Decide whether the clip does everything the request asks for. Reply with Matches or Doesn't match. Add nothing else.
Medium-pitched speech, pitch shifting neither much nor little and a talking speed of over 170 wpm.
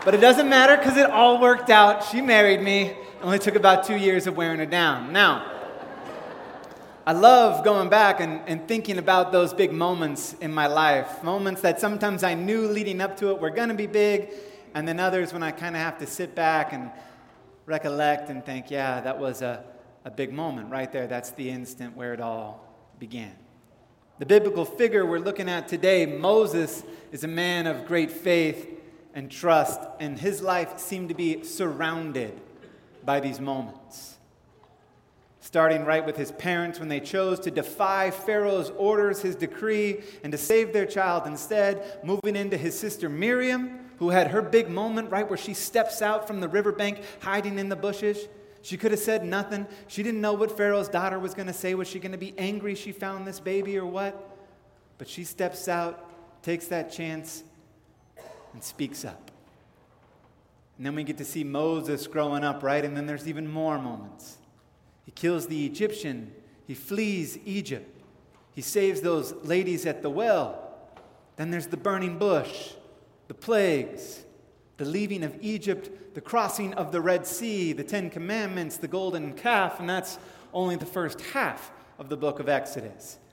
Matches